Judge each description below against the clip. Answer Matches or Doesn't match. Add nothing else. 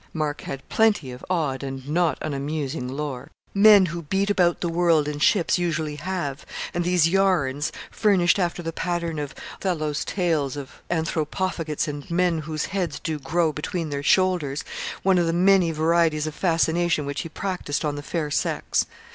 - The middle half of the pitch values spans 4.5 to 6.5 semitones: Doesn't match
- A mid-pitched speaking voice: Matches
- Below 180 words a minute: Matches